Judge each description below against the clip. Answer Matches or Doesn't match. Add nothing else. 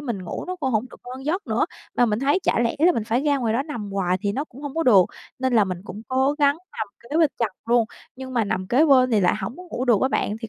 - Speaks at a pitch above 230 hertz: Matches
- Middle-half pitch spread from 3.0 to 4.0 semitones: Doesn't match